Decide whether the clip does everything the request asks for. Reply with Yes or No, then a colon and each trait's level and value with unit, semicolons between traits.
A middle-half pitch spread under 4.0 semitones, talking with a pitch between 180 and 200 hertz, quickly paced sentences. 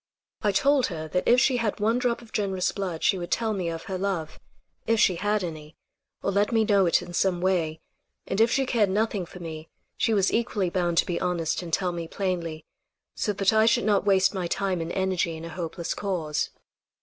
Yes: average, 3.5 semitones; high, 190 Hz; fast, 220 wpm